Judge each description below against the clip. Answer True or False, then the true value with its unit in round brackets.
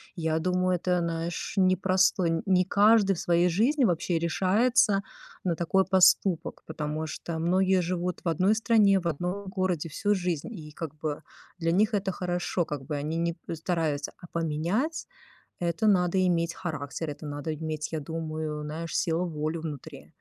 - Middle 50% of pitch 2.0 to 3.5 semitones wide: True (2.9 semitones)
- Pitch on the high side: False (170 Hz)